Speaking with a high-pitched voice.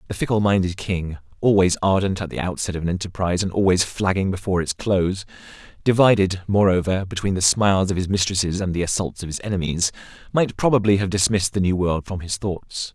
No: very low, 95 Hz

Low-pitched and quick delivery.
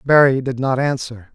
No: low, 130 Hz; average, 180 wpm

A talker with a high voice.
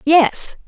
Yes: very high, 300 Hz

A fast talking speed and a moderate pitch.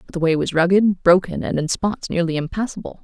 Yes: fast, 215 wpm; medium, 180 Hz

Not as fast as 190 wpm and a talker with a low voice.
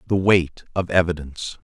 Yes: average, 140 wpm; very low, 85 Hz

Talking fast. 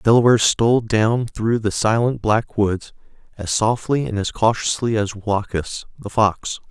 No: average, 160 wpm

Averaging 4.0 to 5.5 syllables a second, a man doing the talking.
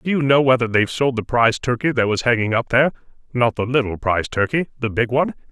No: 6.7 syllables/s; male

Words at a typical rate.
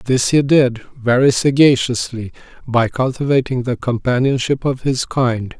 No: slow, 130 wpm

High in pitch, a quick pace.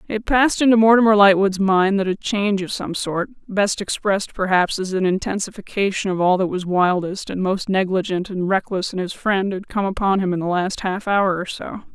Yes: high, 195 Hz; fast, 210 wpm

